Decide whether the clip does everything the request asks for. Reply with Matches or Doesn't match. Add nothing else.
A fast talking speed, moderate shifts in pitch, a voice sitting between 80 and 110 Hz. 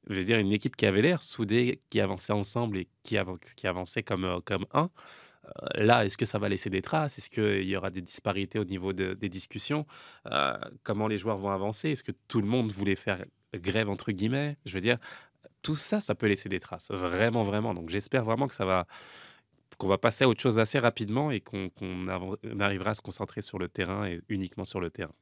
Matches